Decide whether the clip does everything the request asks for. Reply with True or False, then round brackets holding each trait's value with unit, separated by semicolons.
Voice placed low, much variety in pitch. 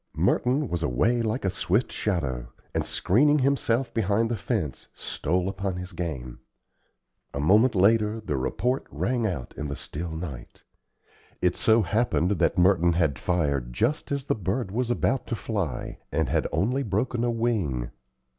True (100 Hz; 6.4 semitones)